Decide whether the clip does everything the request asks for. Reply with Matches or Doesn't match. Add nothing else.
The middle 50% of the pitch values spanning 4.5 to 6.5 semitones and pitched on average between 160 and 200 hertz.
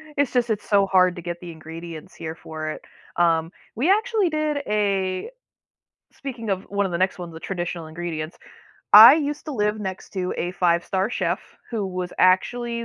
Matches